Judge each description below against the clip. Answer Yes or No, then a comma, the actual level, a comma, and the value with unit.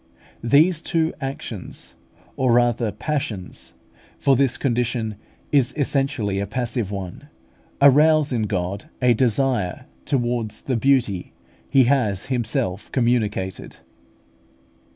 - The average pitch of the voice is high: No, low, 120 Hz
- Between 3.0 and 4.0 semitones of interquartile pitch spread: No, average, 4.5 semitones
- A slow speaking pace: Yes, slow, 105 wpm